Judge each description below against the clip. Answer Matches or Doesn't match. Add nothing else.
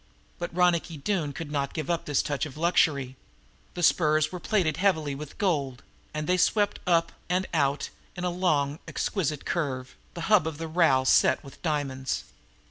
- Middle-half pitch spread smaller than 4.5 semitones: Matches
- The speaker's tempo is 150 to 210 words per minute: Matches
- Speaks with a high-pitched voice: Doesn't match